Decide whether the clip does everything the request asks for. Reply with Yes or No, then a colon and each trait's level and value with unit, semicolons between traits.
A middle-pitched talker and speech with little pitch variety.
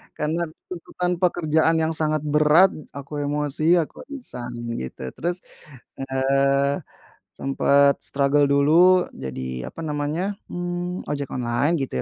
No: medium, 150 Hz; average, 3.8 semitones